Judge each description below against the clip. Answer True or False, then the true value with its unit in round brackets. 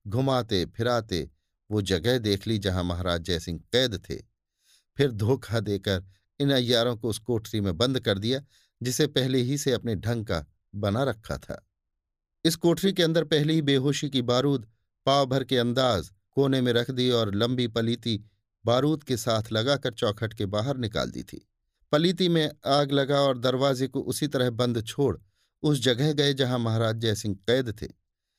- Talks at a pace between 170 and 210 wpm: True (175 wpm)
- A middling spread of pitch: True (4.8 semitones)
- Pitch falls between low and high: False (120 Hz)